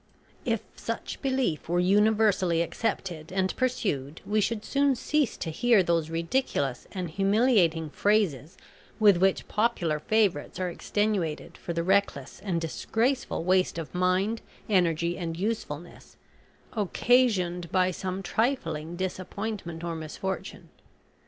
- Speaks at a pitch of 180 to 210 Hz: Yes, medium, 185 Hz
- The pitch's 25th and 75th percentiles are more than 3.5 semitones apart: Yes, average, 4.3 semitones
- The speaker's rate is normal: No, slow, 120 wpm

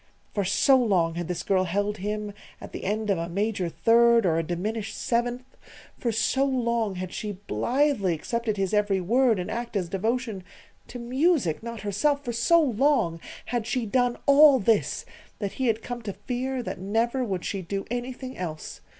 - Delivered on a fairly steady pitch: No, average, 4.1 semitones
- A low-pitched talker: No, high, 220 Hz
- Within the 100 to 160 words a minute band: No, average, 185 wpm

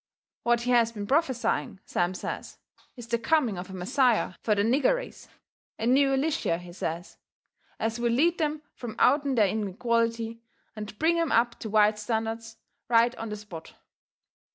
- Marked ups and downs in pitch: No, average, 3.6 semitones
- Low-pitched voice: No, high, 230 Hz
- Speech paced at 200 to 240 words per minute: No, average, 170 wpm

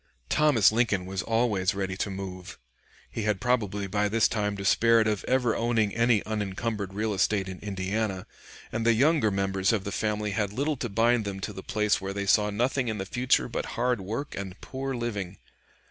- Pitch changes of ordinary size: Yes, average, 3.0 semitones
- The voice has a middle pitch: No, low, 105 Hz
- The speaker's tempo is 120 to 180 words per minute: No, average, 190 wpm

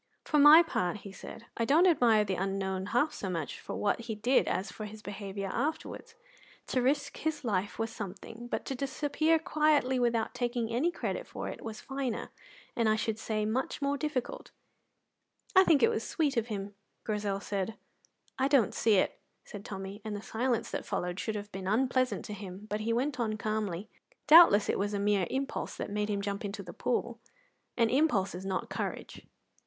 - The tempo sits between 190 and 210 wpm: Yes, average, 195 wpm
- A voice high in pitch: Yes, high, 220 Hz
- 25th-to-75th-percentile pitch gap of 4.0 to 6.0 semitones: Yes, average, 4.7 semitones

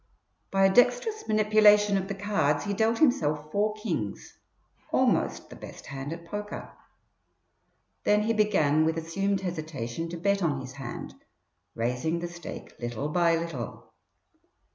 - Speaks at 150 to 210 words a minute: No, average, 140 wpm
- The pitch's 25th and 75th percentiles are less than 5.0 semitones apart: No, wide, 5.6 semitones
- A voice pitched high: No, medium, 175 Hz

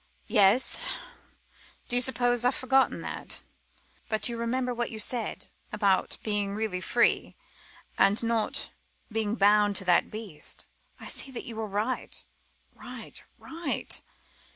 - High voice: Yes, high, 225 Hz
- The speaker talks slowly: Yes, slow, 130 wpm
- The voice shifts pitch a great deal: No, average, 2.9 semitones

